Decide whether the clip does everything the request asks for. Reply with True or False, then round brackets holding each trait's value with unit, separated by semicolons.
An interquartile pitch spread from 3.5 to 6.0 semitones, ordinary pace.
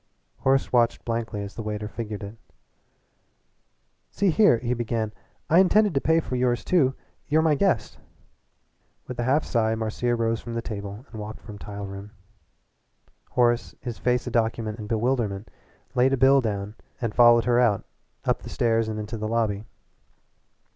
False (2.8 semitones; 170 wpm)